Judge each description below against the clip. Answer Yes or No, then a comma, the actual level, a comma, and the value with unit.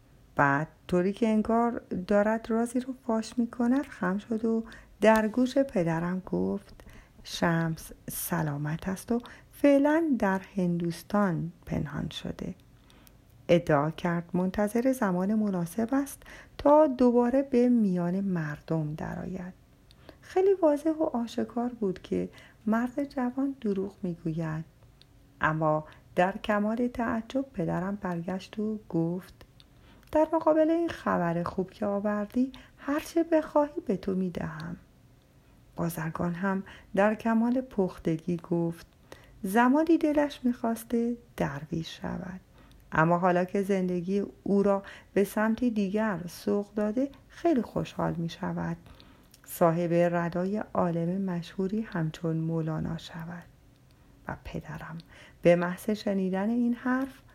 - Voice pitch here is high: Yes, high, 195 Hz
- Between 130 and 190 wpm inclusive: No, average, 115 wpm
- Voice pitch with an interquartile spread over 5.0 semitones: Yes, wide, 5.6 semitones